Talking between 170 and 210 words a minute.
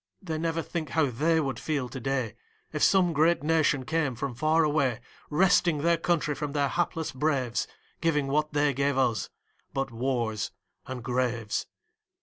No: average, 160 wpm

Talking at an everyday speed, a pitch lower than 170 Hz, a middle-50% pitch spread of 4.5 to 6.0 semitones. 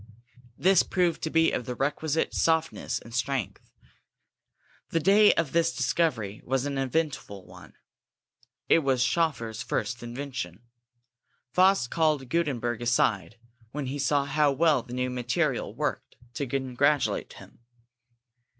No: slow, 130 wpm; low, 135 Hz; average, 4.9 semitones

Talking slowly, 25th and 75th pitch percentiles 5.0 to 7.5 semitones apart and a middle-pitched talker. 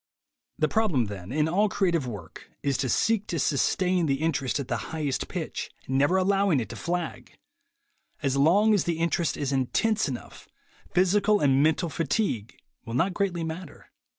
No: average, 165 wpm; wide, 5.6 semitones; medium, 160 Hz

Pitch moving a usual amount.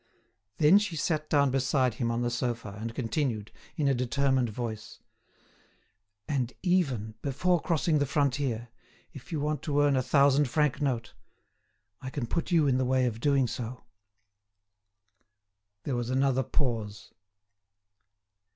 Yes: average, 3.4 semitones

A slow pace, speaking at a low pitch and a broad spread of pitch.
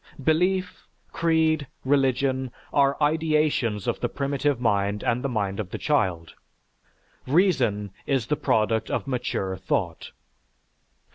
Yes: slow, 120 wpm; low, 130 Hz; wide, 6.2 semitones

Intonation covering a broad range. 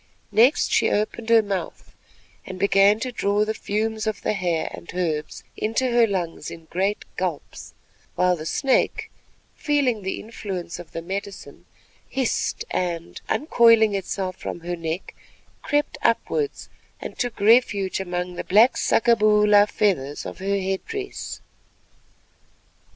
No: average, 3.9 semitones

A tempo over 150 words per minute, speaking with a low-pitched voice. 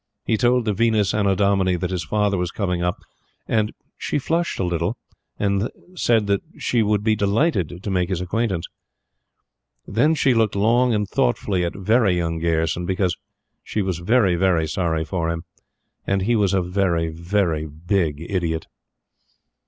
Yes: average, 160 wpm; very low, 95 Hz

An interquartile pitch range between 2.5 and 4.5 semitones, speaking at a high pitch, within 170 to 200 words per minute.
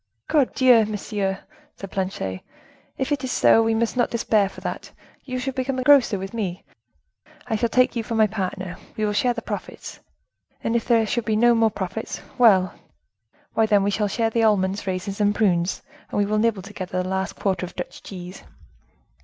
Yes: average, 3.3 semitones; high, 215 Hz; average, 195 wpm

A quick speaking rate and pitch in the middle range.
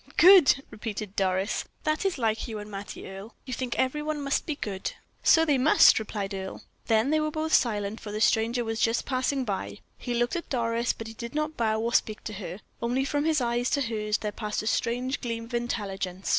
No: fast, 220 wpm; high, 230 Hz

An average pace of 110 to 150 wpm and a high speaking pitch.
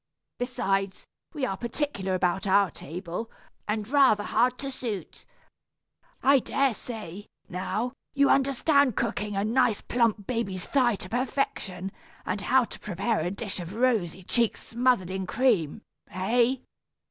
Yes: slow, 135 wpm; high, 220 Hz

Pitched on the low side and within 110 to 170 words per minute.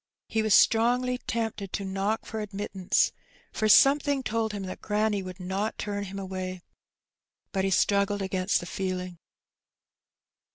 No: high, 200 Hz; average, 150 wpm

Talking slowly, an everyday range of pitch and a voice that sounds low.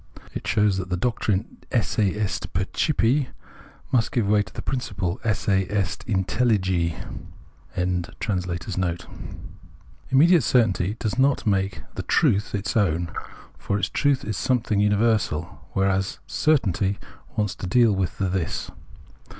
Yes: slow, 125 wpm; average, 3.5 semitones; low, 100 Hz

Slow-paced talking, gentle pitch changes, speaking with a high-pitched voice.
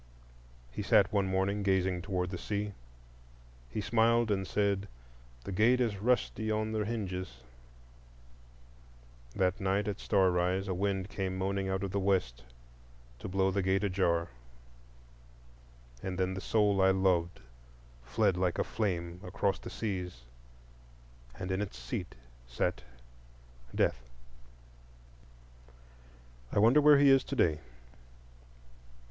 No: slow, 130 wpm; narrow, 2.1 semitones; very low, 95 Hz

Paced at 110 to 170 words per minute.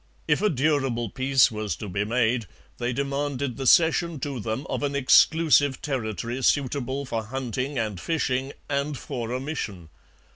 Yes: average, 155 wpm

